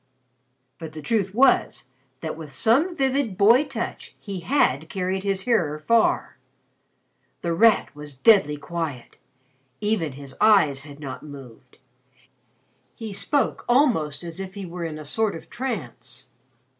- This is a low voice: No, medium, 180 Hz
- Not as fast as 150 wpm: Yes, average, 140 wpm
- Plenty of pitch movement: Yes, wide, 7.0 semitones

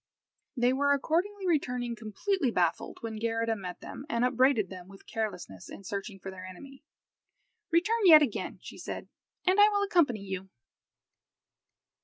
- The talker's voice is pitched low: No, high, 240 Hz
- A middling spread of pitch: No, wide, 7.9 semitones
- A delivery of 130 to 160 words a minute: Yes, average, 150 wpm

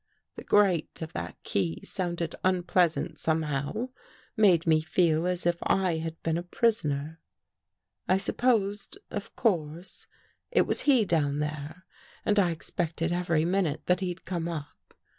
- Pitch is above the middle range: No, medium, 170 Hz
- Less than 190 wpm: Yes, average, 150 wpm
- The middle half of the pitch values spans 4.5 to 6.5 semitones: No, average, 3.0 semitones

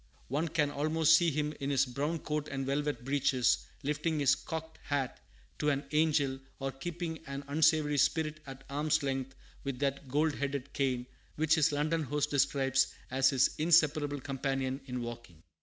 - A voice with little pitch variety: Yes, narrow, 2.2 semitones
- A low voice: No, medium, 145 Hz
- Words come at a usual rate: Yes, average, 165 wpm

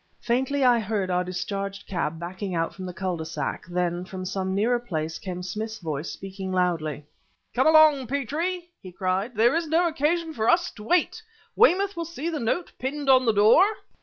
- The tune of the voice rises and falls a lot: Yes, wide, 8.1 semitones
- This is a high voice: Yes, high, 215 Hz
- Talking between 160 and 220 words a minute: Yes, average, 190 wpm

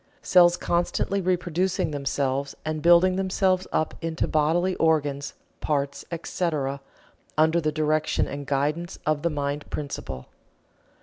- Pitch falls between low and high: Yes, medium, 155 Hz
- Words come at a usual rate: No, slow, 120 wpm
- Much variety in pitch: No, average, 3.4 semitones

